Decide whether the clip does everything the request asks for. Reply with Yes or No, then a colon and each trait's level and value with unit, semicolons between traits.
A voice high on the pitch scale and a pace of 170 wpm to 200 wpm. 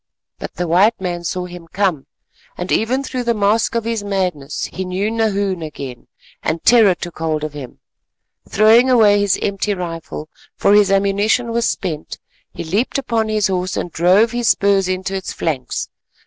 Yes: high, 195 Hz; average, 175 wpm